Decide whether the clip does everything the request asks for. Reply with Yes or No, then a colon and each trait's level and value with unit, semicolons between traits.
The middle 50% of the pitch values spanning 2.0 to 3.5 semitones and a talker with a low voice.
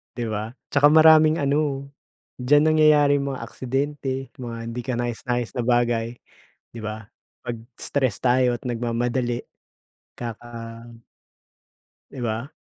Yes: average, 3.0 semitones; low, 125 Hz